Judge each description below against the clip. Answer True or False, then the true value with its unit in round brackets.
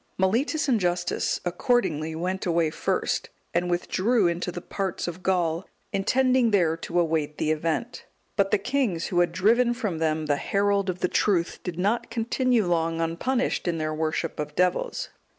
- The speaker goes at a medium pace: True (170 wpm)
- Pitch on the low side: False (180 Hz)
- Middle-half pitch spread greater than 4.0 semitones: True (4.5 semitones)